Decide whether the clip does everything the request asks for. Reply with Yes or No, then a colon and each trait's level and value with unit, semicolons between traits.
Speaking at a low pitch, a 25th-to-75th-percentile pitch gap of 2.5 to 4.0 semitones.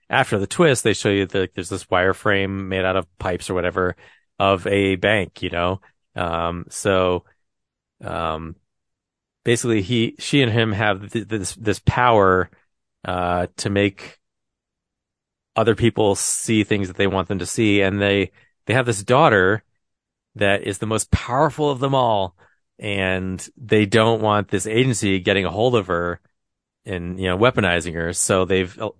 Yes: low, 100 Hz; average, 3.2 semitones